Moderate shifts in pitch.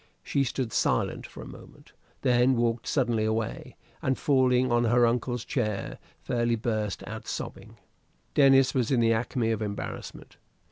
No: narrow, 2.3 semitones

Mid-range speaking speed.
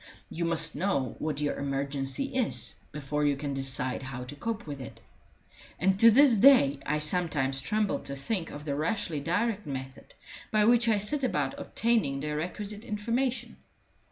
Yes: average, 165 wpm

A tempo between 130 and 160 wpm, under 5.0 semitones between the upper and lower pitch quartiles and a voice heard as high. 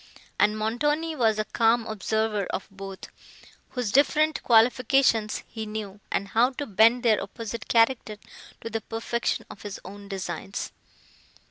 Yes: average, 140 wpm; narrow, 2.6 semitones; high, 220 Hz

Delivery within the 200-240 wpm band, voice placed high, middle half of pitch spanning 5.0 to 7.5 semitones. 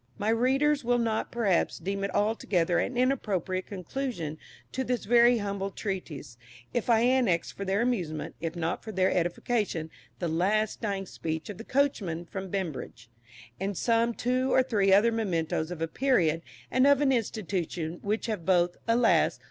No: average, 170 wpm; high, 200 Hz; wide, 5.5 semitones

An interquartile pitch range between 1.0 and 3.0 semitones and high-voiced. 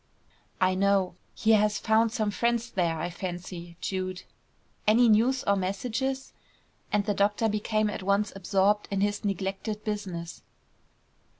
Yes: narrow, 2.5 semitones; high, 205 Hz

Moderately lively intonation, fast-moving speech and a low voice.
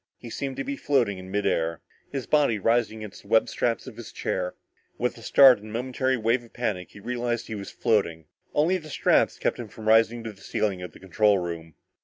Yes: average, 3.7 semitones; fast, 235 wpm; low, 110 Hz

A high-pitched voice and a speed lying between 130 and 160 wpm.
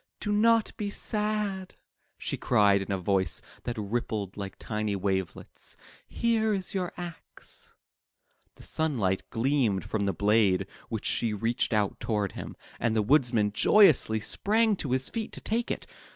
No: low, 115 Hz; average, 150 wpm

